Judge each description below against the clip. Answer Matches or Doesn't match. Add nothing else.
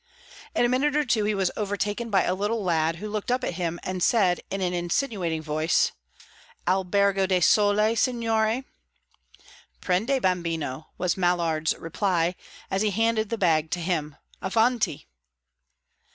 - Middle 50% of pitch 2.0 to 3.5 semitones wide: Doesn't match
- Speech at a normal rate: Matches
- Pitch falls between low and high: Doesn't match